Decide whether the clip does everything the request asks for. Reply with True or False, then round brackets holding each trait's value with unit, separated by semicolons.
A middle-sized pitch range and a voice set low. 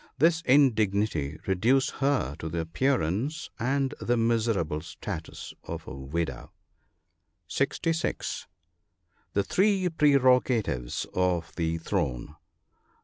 False (9.0 semitones; 110 Hz)